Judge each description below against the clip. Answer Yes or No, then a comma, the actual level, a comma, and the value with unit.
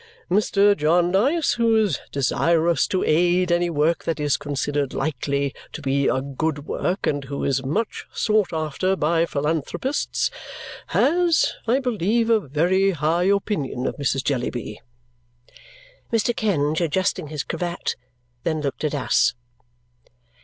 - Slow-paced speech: Yes, slow, 130 wpm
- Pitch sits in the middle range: Yes, medium, 165 Hz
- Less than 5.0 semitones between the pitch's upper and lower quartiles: No, wide, 5.6 semitones